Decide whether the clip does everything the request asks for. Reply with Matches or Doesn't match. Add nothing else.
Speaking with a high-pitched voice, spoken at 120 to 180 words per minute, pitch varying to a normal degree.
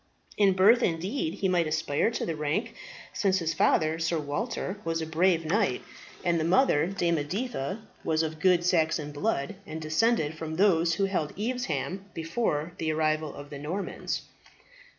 Doesn't match